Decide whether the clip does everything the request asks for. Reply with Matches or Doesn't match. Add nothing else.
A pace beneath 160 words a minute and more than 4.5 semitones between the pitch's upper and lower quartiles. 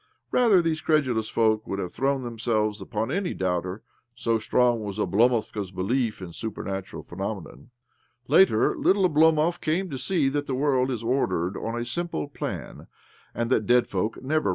Doesn't match